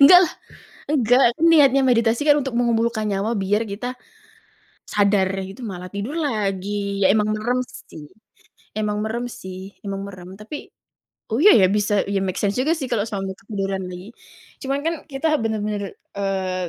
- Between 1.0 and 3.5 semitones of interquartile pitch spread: No, average, 3.9 semitones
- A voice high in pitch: Yes, high, 210 Hz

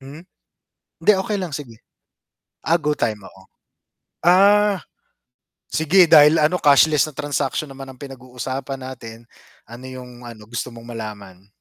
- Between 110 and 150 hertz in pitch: Yes, low, 135 Hz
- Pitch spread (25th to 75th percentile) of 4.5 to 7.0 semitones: Yes, average, 4.8 semitones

